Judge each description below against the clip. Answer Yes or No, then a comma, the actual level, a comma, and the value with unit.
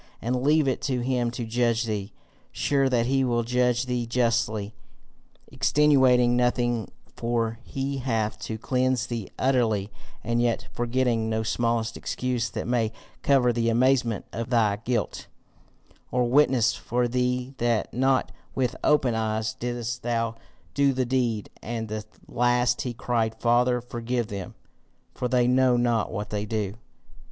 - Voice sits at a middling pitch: No, low, 120 Hz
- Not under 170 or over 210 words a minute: No, average, 145 wpm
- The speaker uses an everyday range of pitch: No, narrow, 1.7 semitones